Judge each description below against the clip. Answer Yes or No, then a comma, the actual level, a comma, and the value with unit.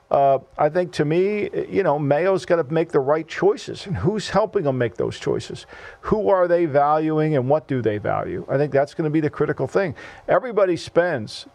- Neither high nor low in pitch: Yes, medium, 155 Hz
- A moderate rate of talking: No, fast, 215 wpm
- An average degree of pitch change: Yes, average, 4.0 semitones